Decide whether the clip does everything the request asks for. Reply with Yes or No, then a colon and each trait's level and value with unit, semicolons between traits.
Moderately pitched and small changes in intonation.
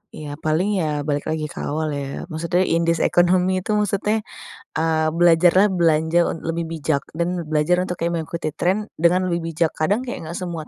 Yes: medium, 170 Hz; narrow, 2.3 semitones